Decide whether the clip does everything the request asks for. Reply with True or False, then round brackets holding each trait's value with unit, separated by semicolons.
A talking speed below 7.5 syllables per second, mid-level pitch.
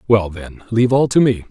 False (5.7 syllables/s; 110 Hz)